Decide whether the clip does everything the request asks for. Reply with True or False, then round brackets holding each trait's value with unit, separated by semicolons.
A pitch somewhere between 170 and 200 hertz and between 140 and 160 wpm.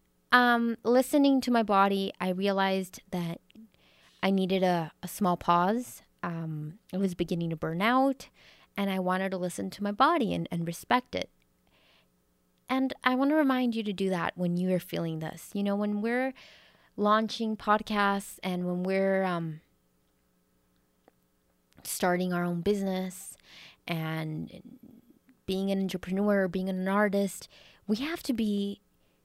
True (190 Hz; 150 wpm)